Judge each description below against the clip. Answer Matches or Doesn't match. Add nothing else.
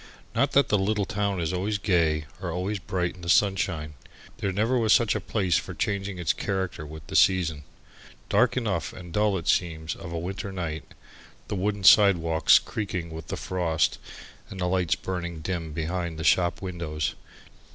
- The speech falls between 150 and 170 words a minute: Doesn't match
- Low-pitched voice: Matches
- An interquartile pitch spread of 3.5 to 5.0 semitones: Doesn't match